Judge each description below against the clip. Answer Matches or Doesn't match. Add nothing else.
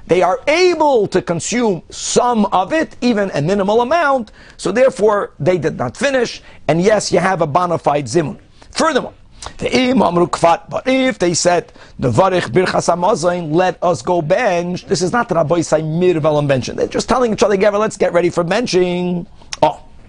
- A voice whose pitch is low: Doesn't match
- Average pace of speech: Matches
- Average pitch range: Matches